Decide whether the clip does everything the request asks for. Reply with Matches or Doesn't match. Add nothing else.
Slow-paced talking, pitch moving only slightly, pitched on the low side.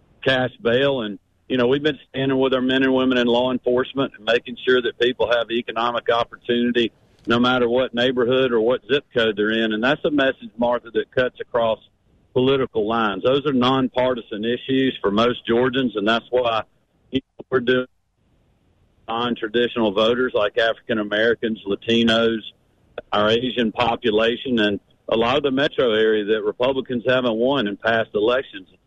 Doesn't match